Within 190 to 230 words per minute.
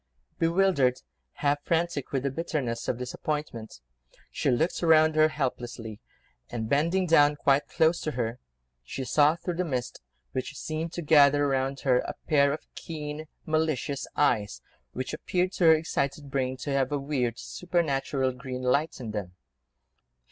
No: average, 155 wpm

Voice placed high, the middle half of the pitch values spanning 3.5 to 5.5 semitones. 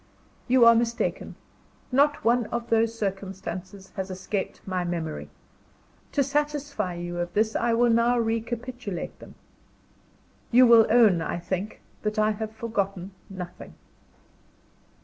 Yes: high, 220 Hz; average, 3.8 semitones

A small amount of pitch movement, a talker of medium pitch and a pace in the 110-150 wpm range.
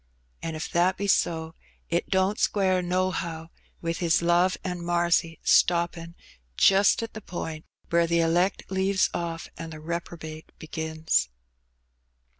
Yes: narrow, 2.0 semitones; medium, 170 Hz; average, 140 wpm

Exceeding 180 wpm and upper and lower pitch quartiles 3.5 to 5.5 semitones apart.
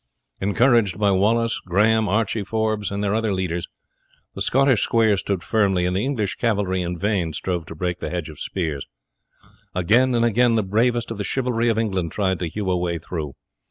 Yes: average, 195 wpm; average, 4.0 semitones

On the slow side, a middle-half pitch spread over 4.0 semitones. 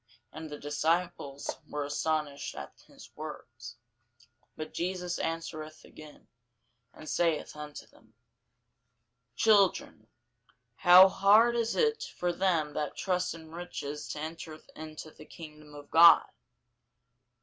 No: slow, 115 wpm; average, 3.0 semitones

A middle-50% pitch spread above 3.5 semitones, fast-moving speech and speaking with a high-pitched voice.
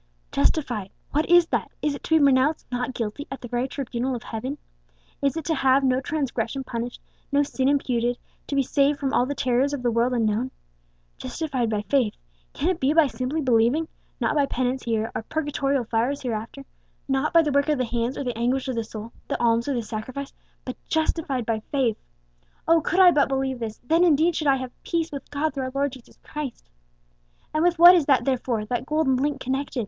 No: average, 3.2 semitones; fast, 215 wpm; very high, 265 Hz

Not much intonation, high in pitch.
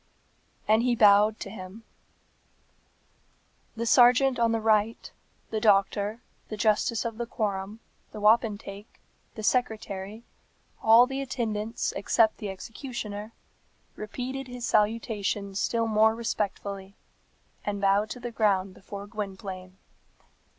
Yes: narrow, 2.3 semitones; high, 215 Hz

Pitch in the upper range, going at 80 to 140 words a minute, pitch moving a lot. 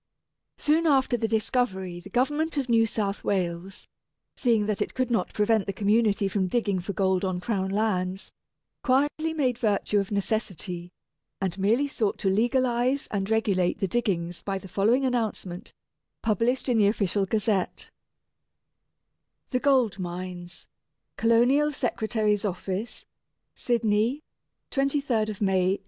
No: high, 215 Hz; slow, 135 wpm; average, 4.1 semitones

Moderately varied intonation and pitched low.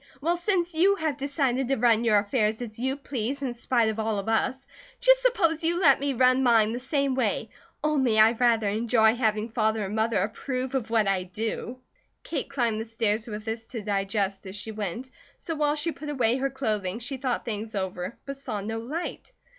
No: average, 4.1 semitones; high, 235 Hz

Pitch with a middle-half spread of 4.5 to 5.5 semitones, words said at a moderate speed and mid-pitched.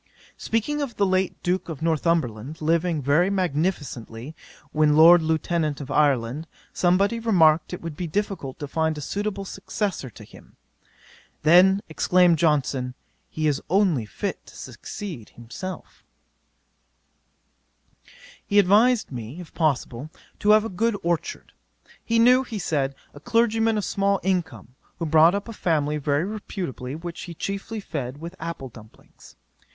Yes: average, 5.1 semitones; average, 145 wpm; medium, 170 Hz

